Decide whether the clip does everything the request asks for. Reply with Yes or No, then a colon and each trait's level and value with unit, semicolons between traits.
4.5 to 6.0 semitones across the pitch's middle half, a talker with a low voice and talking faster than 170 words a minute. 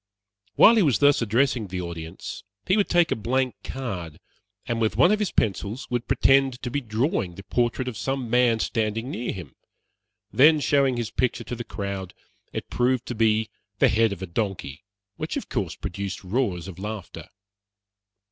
Yes: average, 4.9 semitones; low, 115 Hz; average, 180 wpm